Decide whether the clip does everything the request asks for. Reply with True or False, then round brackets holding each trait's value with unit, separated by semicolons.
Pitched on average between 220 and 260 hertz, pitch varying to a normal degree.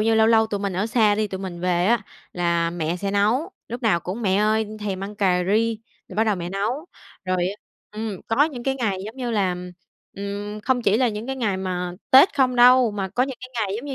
False (210 Hz; 3.9 semitones)